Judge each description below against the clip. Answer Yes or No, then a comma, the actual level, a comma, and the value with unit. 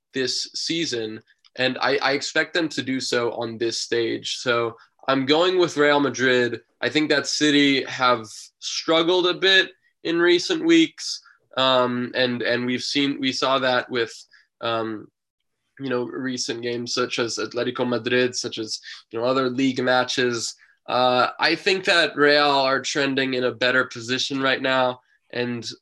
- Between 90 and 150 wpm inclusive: No, average, 160 wpm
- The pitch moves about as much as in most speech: Yes, average, 3.0 semitones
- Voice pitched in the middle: No, low, 130 Hz